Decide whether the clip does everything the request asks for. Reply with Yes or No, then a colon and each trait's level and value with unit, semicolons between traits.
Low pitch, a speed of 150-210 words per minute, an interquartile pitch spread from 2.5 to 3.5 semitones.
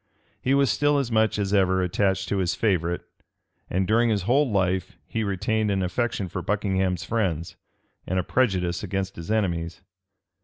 Yes: very low, 95 Hz; average, 165 wpm; average, 3.2 semitones